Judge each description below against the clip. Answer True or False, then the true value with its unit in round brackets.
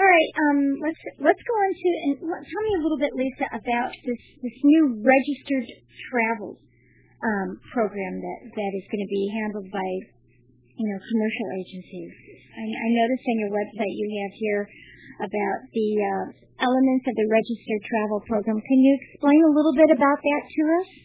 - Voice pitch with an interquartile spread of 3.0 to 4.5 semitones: False (5.6 semitones)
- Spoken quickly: False (180 wpm)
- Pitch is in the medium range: False (230 Hz)